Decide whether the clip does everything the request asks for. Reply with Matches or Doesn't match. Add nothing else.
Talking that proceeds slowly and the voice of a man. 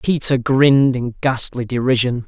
Matches